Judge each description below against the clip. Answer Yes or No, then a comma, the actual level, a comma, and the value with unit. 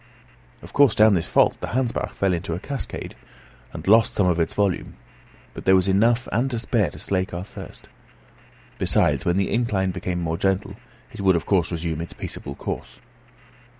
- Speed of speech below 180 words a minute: No, average, 185 wpm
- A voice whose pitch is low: Yes, very low, 95 Hz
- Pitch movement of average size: Yes, average, 3.9 semitones